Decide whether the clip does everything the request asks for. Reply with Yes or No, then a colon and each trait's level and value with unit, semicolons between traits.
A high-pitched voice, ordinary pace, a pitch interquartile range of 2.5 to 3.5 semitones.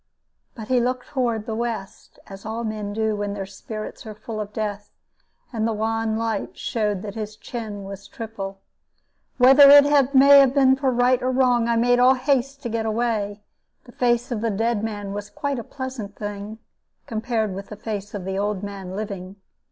Yes: high, 220 Hz; average, 190 wpm; average, 3.1 semitones